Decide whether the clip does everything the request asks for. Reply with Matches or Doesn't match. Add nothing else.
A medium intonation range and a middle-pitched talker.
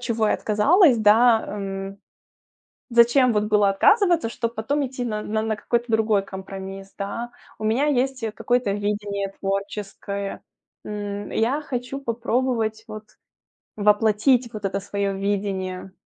Doesn't match